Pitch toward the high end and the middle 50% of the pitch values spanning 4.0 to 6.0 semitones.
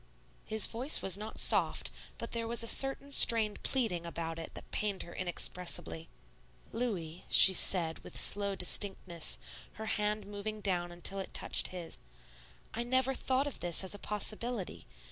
Yes: high, 205 Hz; average, 4.7 semitones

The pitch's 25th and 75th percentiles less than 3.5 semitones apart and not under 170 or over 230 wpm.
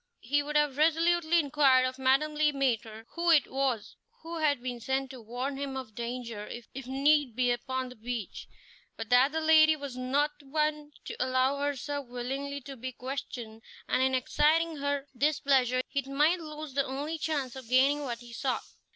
Yes: average, 2.9 semitones; average, 180 wpm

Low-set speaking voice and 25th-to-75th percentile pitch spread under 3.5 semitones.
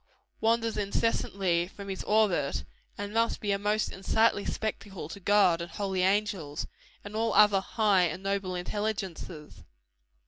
No: high, 200 Hz; narrow, 2.5 semitones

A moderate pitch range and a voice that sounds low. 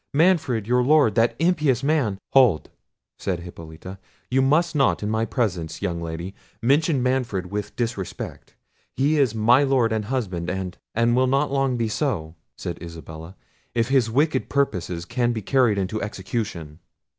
No: wide, 6.3 semitones; low, 115 Hz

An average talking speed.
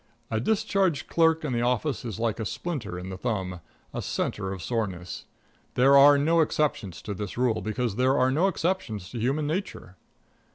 Yes: average, 180 wpm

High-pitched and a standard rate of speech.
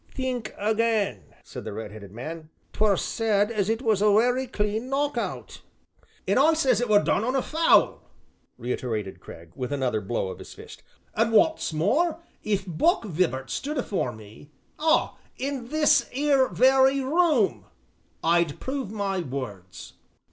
Yes: high, 215 Hz; average, 160 wpm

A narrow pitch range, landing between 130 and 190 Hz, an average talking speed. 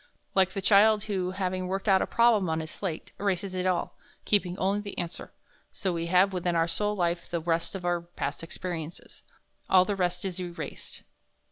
Yes: narrow, 2.2 semitones; medium, 185 Hz; average, 195 wpm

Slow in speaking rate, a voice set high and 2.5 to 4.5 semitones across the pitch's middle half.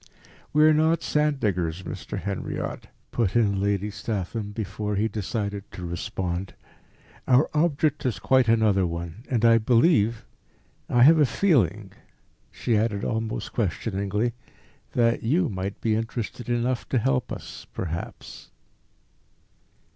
No: slow, 130 wpm; low, 110 Hz; average, 3.9 semitones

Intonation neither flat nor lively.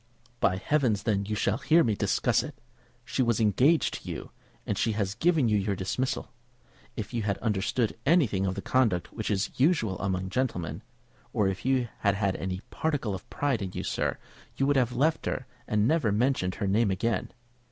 Yes: average, 5.0 semitones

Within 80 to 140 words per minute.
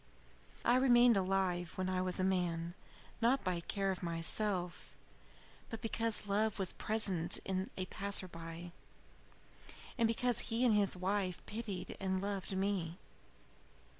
Yes: slow, 135 wpm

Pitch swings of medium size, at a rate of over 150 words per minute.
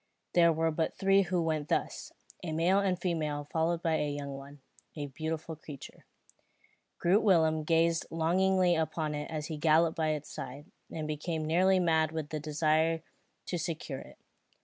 No: narrow, 1.8 semitones; average, 170 wpm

